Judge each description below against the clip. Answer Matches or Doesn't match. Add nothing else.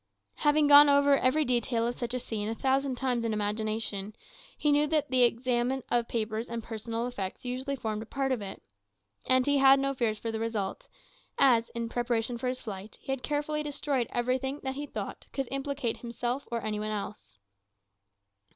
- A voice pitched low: Doesn't match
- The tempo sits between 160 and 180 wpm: Doesn't match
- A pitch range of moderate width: Matches